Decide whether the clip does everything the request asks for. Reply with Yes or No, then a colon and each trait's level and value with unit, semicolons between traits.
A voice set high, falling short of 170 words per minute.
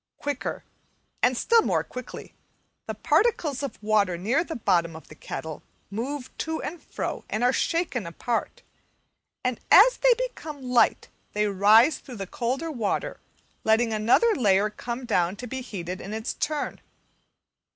Yes: high, 245 Hz; average, 150 wpm